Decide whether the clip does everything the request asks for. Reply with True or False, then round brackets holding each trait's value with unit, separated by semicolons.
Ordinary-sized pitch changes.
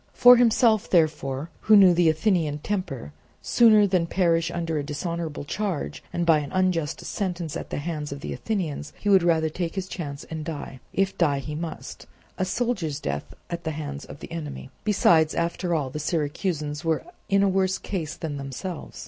True (4.0 semitones)